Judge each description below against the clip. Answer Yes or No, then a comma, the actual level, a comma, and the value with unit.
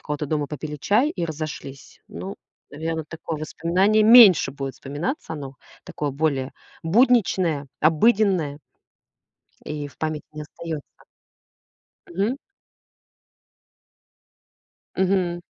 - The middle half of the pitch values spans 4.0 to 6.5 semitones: Yes, average, 4.4 semitones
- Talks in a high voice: No, medium, 160 Hz